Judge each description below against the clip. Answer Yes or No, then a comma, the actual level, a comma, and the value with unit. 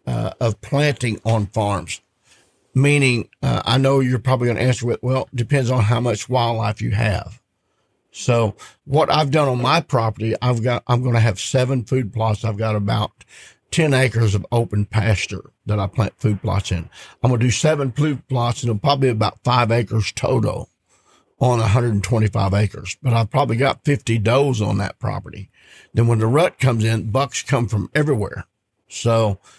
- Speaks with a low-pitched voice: Yes, low, 115 Hz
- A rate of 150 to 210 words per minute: Yes, average, 185 wpm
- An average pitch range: Yes, average, 3.3 semitones